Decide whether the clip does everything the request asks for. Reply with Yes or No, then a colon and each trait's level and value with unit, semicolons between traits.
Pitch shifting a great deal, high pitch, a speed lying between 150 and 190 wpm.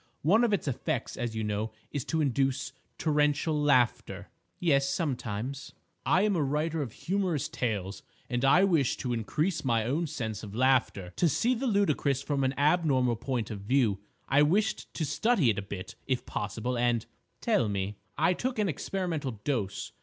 No: wide, 5.8 semitones; low, 135 Hz; average, 170 wpm